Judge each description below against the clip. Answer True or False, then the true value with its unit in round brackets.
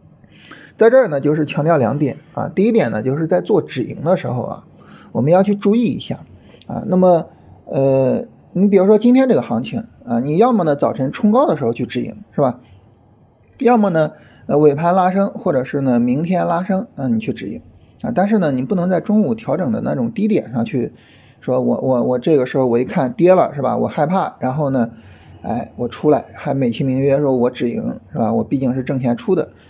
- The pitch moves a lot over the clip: True (7.5 semitones)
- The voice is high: False (150 Hz)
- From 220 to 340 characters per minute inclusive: True (300 characters per minute)